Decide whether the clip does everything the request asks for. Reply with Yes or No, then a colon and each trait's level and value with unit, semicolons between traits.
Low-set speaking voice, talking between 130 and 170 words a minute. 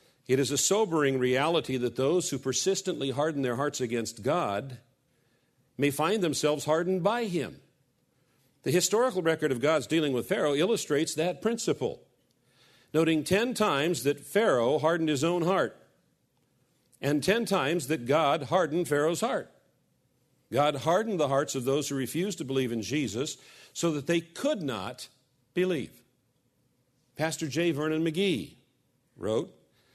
No: medium, 155 Hz; average, 140 wpm